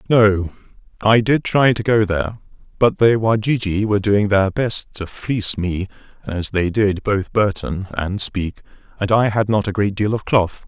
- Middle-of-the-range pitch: No, low, 105 Hz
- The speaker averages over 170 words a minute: Yes, average, 185 wpm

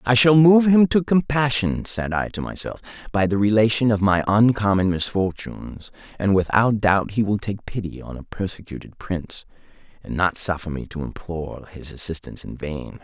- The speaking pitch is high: No, low, 105 Hz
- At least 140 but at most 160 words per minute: No, average, 175 wpm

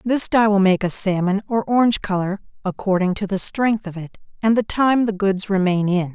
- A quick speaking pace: Yes, fast, 215 wpm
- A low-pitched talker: No, high, 200 Hz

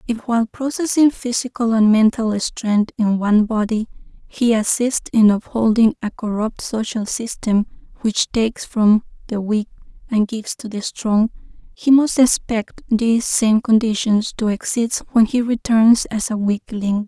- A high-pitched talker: Yes, high, 225 Hz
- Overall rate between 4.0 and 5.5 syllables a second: Yes, 4.5 syllables/s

